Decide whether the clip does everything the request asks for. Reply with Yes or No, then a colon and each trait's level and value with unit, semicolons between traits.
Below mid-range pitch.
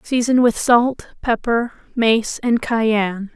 No: high, 230 Hz